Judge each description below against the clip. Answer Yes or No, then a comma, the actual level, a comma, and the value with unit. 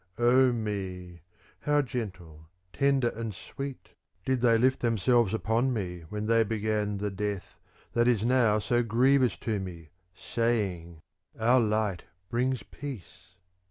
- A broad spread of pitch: No, average, 3.7 semitones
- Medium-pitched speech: No, low, 110 Hz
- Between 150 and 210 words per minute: No, slow, 135 wpm